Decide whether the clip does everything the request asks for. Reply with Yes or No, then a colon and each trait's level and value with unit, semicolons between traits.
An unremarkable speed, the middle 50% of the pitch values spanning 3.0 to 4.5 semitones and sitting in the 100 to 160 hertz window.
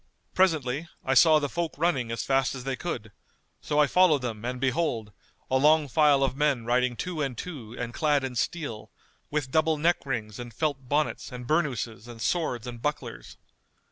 Yes: average, 185 wpm; average, 4.0 semitones; low, 135 Hz